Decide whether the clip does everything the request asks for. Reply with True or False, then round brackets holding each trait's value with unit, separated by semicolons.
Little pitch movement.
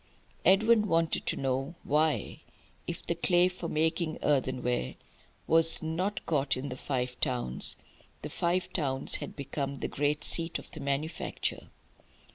False (4.0 semitones)